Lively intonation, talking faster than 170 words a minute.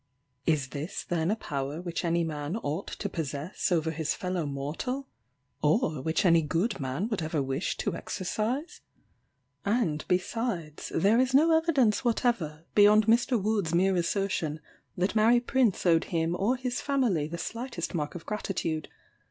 No: wide, 6.1 semitones; average, 155 wpm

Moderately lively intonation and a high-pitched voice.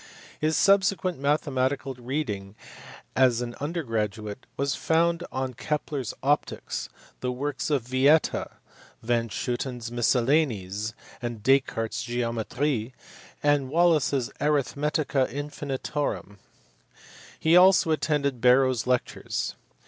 No: average, 3.7 semitones; low, 135 Hz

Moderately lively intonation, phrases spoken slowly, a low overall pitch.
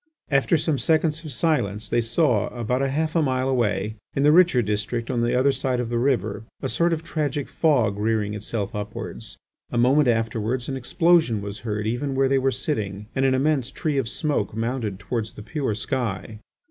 No: average, 4.5 semitones; average, 195 wpm; low, 125 Hz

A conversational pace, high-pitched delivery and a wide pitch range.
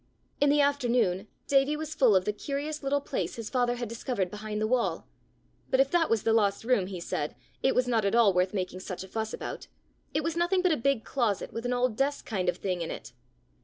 No: fast, 240 wpm; high, 235 Hz; wide, 5.7 semitones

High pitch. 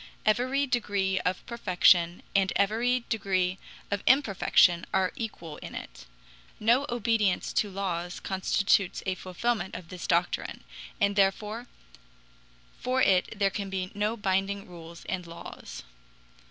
Yes: high, 195 Hz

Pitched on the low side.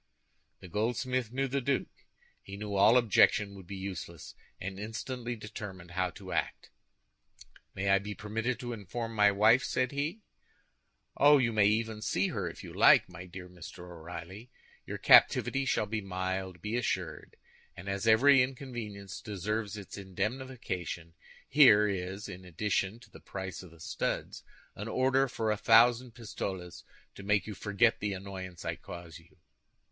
Yes: low, 105 Hz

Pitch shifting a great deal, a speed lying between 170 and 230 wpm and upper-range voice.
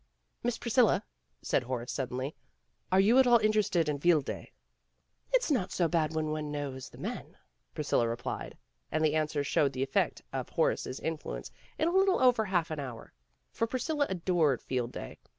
No: wide, 8.1 semitones; average, 180 wpm; medium, 160 Hz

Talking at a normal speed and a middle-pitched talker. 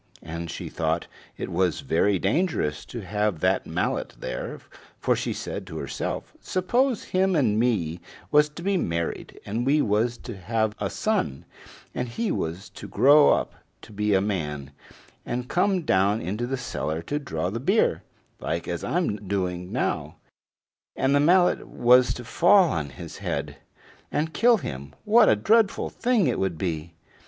No: average, 165 wpm; low, 110 Hz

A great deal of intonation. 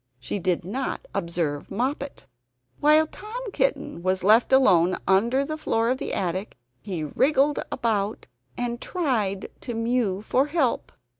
Yes: wide, 6.5 semitones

